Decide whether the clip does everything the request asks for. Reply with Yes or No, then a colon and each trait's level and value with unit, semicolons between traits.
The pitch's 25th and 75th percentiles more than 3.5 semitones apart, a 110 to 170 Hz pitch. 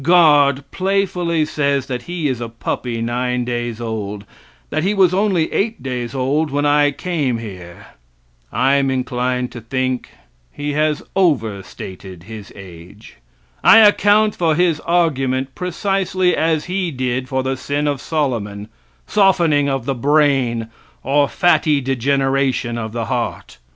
Yes: average, 5.1 semitones; low, 135 Hz